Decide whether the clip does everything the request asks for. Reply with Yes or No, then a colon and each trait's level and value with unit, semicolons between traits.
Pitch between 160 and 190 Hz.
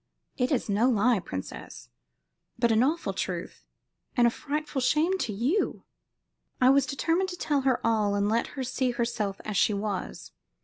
No: high, 245 Hz